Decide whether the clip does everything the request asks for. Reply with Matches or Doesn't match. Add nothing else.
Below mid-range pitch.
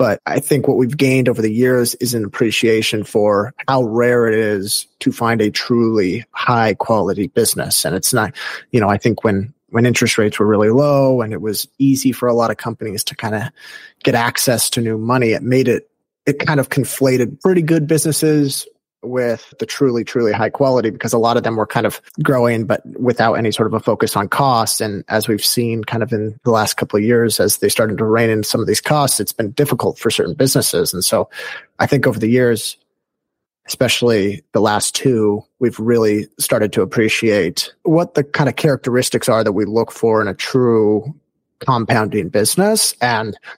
Matches